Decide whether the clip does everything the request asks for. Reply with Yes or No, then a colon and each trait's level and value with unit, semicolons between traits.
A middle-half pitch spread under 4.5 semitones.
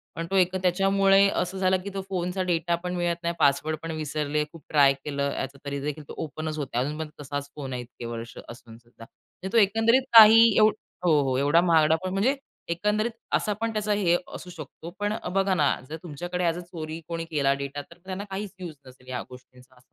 No: average, 4.8 semitones